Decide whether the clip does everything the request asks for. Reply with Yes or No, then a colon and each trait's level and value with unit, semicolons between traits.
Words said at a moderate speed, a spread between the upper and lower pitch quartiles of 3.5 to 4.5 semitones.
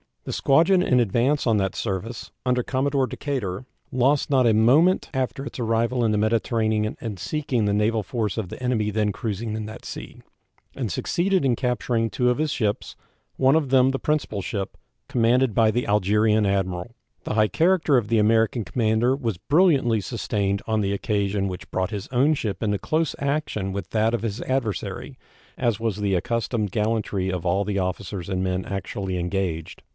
Yes: average, 180 wpm; average, 4.0 semitones